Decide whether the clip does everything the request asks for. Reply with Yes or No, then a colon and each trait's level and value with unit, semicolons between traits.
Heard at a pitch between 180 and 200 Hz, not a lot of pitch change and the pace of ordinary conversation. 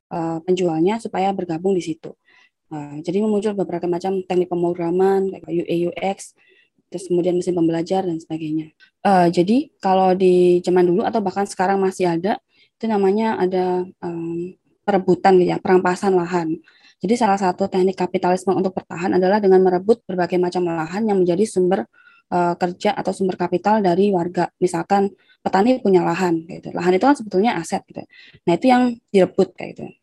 No: medium, 185 Hz; narrow, 2.0 semitones; fast, 150 wpm